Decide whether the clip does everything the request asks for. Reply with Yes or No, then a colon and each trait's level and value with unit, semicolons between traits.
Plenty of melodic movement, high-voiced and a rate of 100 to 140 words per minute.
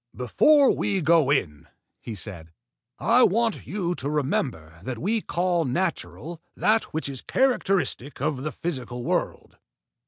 No: wide, 7.5 semitones; medium, 150 Hz; slow, 135 wpm